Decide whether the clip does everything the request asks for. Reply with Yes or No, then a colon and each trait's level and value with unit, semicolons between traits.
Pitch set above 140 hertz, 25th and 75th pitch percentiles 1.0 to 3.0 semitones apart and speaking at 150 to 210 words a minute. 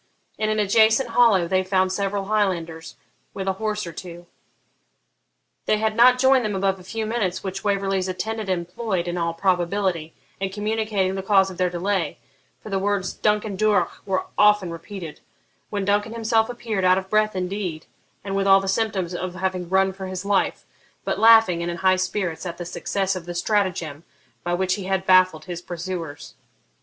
Yes: high, 190 Hz; narrow, 2.5 semitones; average, 185 wpm